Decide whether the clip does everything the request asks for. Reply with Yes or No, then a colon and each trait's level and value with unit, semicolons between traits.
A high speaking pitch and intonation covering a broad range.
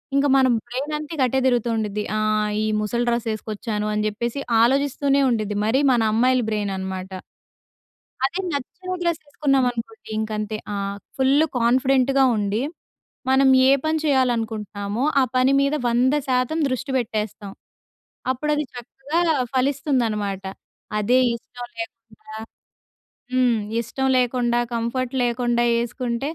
No: high, 245 Hz; average, 3.7 semitones